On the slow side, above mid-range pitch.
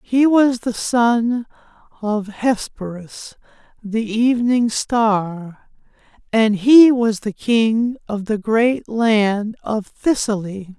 Yes: slow, 110 wpm; high, 225 Hz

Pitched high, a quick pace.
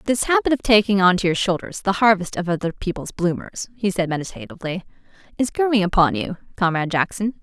No: high, 195 Hz; average, 185 wpm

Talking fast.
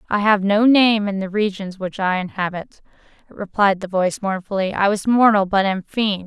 No: average, 190 wpm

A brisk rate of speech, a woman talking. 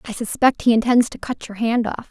Yes: fast, 255 wpm; female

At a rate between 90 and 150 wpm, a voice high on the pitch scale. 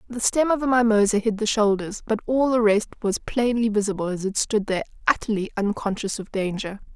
No: average, 200 wpm; high, 215 Hz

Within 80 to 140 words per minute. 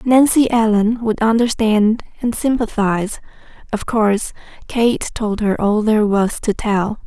Yes: slow, 135 wpm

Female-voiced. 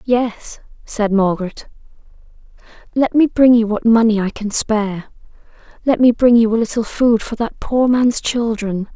Yes: female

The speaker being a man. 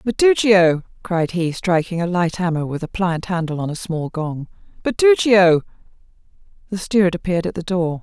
No: female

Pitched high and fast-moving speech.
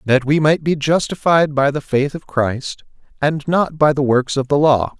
No: medium, 145 Hz; fast, 215 wpm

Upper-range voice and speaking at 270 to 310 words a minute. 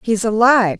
No: high, 225 Hz; fast, 230 wpm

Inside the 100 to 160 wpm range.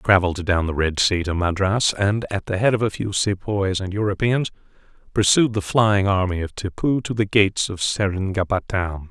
No: average, 190 wpm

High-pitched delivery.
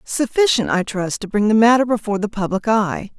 Yes: high, 215 Hz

